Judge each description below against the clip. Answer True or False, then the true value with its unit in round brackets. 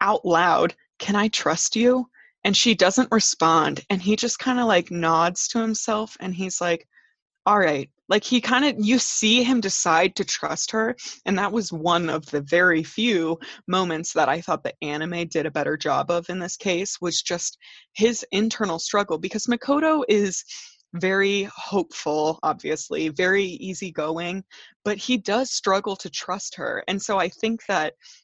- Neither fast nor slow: True (175 wpm)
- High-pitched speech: True (195 Hz)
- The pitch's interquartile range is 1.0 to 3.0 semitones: False (4.5 semitones)